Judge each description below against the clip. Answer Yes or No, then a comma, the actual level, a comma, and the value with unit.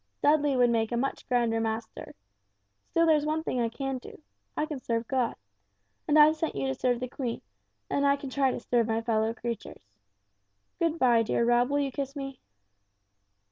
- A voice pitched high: Yes, very high, 250 Hz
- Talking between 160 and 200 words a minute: Yes, average, 190 wpm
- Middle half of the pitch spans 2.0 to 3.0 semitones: No, average, 3.6 semitones